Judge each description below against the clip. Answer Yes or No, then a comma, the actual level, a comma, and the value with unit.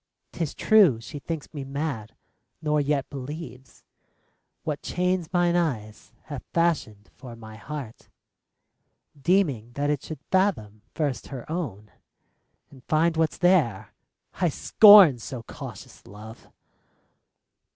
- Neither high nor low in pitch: Yes, medium, 145 Hz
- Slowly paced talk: Yes, slow, 125 wpm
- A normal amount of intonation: No, wide, 6.2 semitones